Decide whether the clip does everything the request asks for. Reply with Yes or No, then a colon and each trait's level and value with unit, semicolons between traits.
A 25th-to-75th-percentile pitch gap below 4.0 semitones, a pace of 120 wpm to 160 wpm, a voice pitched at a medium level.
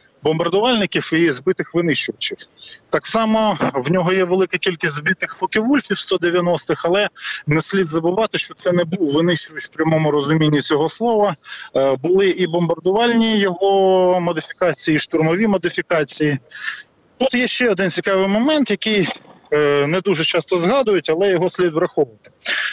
Yes: average, 3.4 semitones; average, 135 wpm; medium, 180 Hz